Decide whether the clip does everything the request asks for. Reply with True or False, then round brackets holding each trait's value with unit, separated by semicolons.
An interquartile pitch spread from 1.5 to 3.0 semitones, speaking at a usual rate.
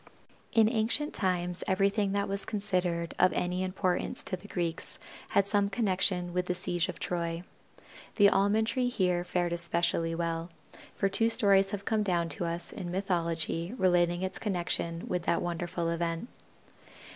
True (2.6 semitones; 155 wpm)